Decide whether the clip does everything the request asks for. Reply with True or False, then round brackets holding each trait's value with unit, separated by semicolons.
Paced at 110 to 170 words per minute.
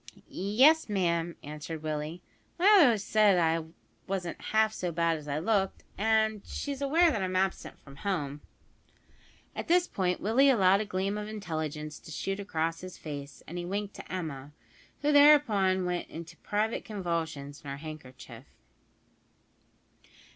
True (155 wpm)